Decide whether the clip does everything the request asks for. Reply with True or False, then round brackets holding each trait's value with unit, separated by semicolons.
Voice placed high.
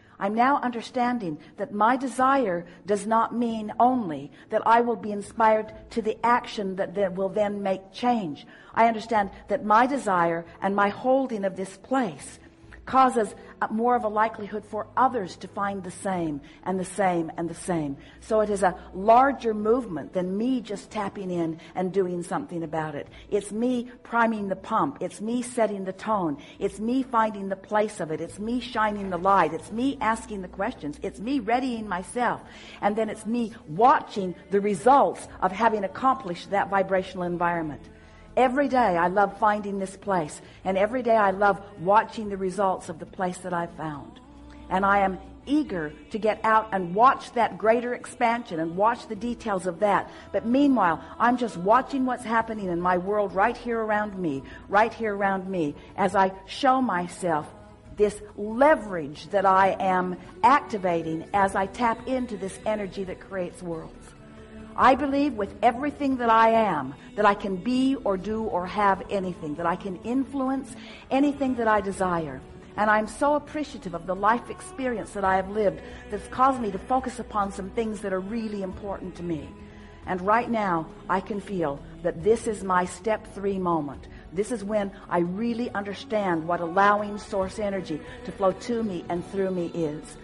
True (205 Hz)